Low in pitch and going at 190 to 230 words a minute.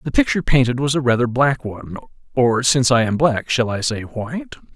Yes: low, 130 Hz; average, 200 wpm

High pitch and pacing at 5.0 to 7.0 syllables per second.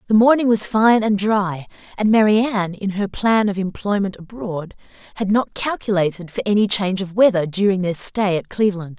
Yes: high, 200 Hz; 5.2 syllables/s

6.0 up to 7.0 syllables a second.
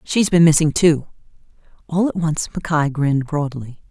No: 5.1 syllables/s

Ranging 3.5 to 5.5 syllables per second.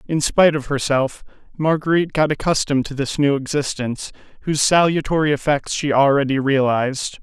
No: 5.9 syllables/s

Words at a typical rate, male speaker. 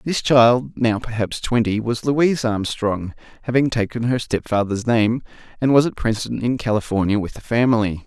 Yes: average, 165 wpm; male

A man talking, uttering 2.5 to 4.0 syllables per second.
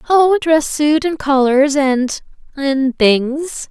No: female; 3.1 syllables/s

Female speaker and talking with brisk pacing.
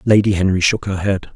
No: male; fast, 220 wpm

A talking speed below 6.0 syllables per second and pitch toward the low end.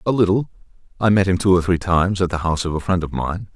No: 6.9 syllables/s; very low, 90 Hz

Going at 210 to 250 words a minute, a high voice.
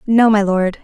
Yes: fast, 215 wpm; high, 210 Hz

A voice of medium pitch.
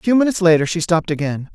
Yes: medium, 175 Hz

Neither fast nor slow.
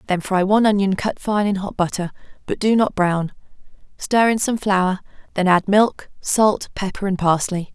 Yes: average, 185 wpm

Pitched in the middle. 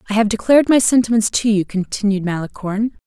No: high, 215 Hz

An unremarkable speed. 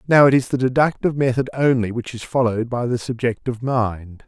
Yes: average, 195 wpm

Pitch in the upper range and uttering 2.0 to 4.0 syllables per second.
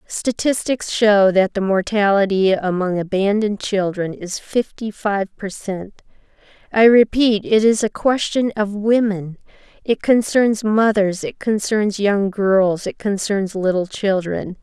Yes: high, 205 Hz; 3.9 syllables/s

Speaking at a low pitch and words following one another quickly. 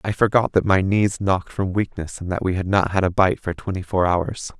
Yes: very low, 95 Hz; fast, 260 wpm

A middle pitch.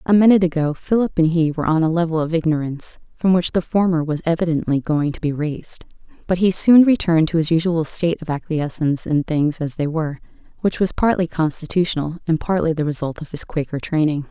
Yes: medium, 165 Hz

